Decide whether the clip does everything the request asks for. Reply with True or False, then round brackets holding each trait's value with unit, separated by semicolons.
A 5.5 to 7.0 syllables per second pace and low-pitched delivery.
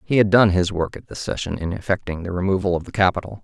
True (6.6 syllables/s; 95 Hz)